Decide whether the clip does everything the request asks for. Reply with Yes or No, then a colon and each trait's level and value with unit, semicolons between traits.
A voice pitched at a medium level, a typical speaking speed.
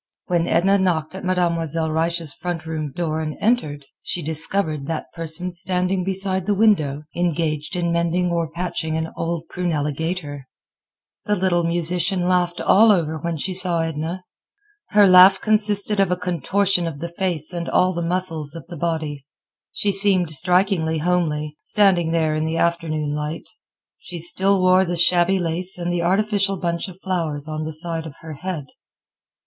Yes: medium, 170 Hz; average, 165 wpm